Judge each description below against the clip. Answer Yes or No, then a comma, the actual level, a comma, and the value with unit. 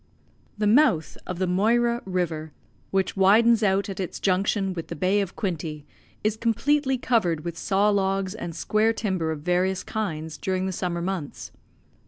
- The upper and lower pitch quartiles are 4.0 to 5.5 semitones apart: No, average, 3.5 semitones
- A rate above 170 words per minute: No, average, 165 wpm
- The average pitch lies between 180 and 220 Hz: Yes, high, 190 Hz